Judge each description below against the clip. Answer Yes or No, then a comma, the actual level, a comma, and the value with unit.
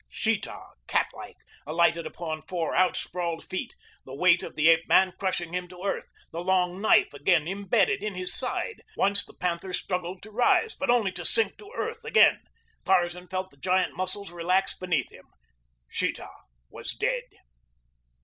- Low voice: No, medium, 180 Hz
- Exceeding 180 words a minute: No, average, 165 wpm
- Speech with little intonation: Yes, narrow, 2.1 semitones